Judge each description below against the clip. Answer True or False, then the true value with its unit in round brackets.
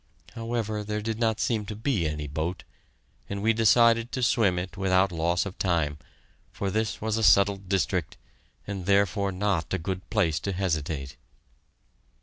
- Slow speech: False (160 wpm)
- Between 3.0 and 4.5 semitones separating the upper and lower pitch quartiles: True (3.6 semitones)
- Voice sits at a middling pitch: False (100 Hz)